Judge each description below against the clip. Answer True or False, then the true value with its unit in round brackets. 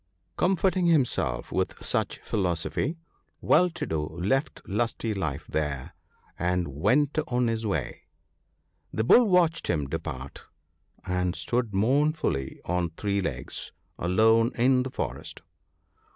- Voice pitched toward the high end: False (105 Hz)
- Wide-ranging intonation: True (7.7 semitones)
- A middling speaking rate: False (120 wpm)